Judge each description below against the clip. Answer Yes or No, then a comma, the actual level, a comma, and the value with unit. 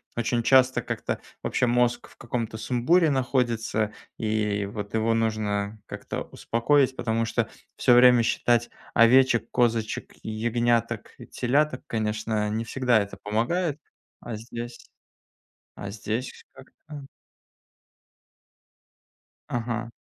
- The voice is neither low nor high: No, low, 115 Hz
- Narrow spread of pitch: Yes, narrow, 2.1 semitones